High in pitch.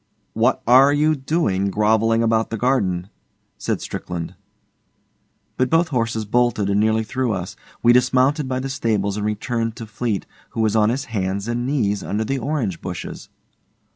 No: low, 115 Hz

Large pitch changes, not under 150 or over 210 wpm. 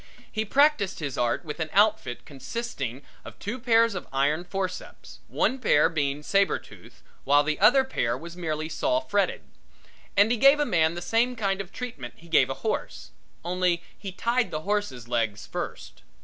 Yes: wide, 7.2 semitones; average, 175 wpm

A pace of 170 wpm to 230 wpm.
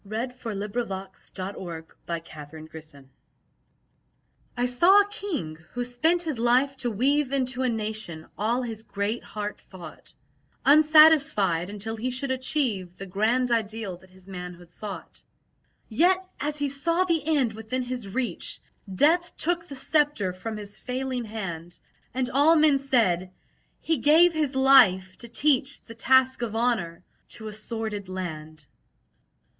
No: average, 150 wpm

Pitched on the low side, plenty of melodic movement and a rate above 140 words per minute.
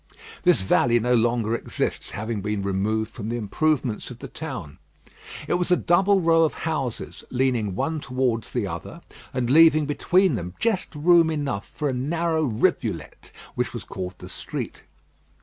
Yes: low, 130 Hz; wide, 6.6 semitones; average, 165 wpm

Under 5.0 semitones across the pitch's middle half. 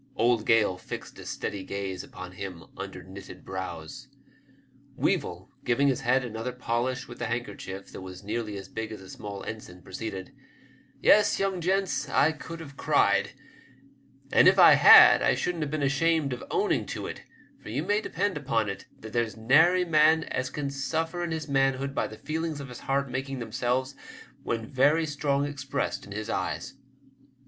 No: wide, 5.6 semitones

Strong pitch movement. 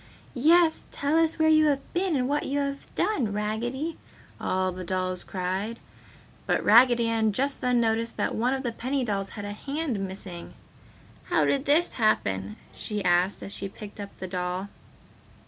Yes: wide, 6.2 semitones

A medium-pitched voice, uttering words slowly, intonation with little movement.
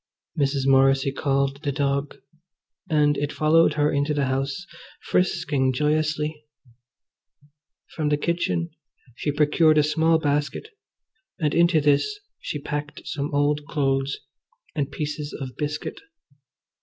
Yes: medium, 150 Hz; slow, 120 wpm; narrow, 1.7 semitones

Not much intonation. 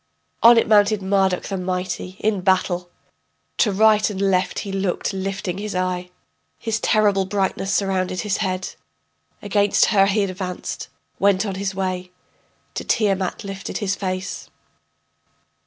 Yes: narrow, 1.7 semitones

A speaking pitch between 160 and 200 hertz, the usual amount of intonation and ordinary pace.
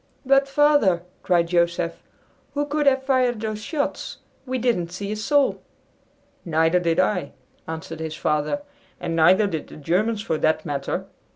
No: medium, 185 Hz; wide, 7.7 semitones; average, 155 wpm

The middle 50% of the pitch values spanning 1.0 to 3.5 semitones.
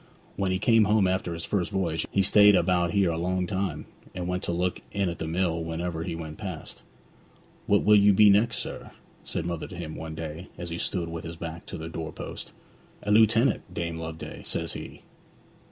Yes: average, 3.2 semitones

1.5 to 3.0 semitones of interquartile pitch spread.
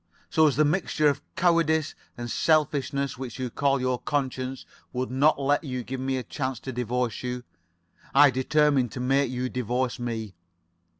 Yes: narrow, 2.5 semitones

